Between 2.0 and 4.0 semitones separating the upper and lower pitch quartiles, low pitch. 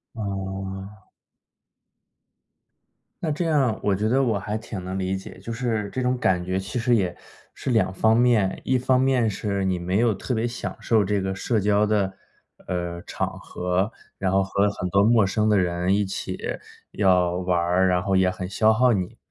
Yes: average, 3.3 semitones; low, 100 Hz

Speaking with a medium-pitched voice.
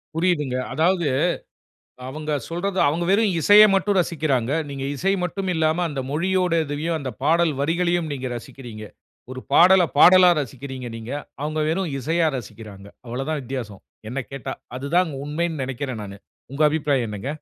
Yes: medium, 150 Hz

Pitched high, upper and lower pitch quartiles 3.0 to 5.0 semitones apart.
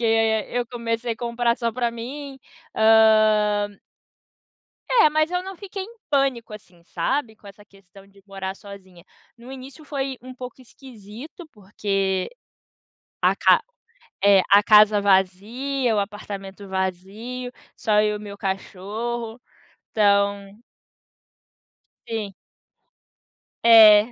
Yes: high, 215 Hz; average, 3.7 semitones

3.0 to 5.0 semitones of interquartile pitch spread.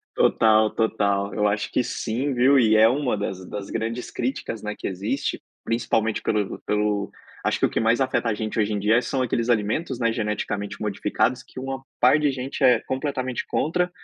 Yes: average, 3.6 semitones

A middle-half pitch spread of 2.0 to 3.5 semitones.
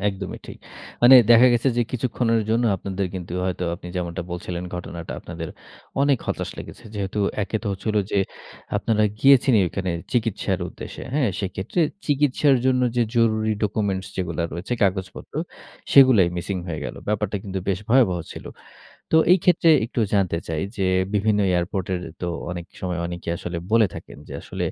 No: average, 4.8 semitones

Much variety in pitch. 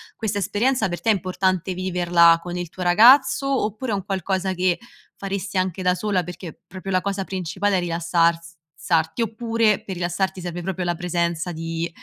No: narrow, 2.4 semitones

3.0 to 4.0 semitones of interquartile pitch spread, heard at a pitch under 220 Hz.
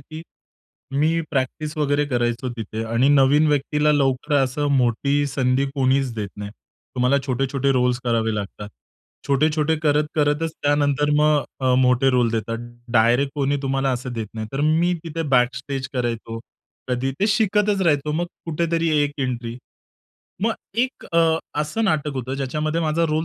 Yes: average, 3.4 semitones; medium, 140 Hz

